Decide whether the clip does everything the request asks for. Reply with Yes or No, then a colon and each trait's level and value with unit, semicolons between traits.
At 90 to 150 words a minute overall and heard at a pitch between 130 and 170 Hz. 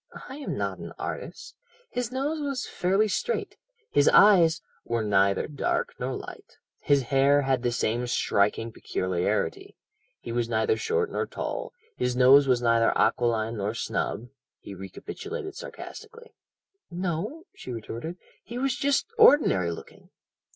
Yes: average, 145 wpm; medium, 140 Hz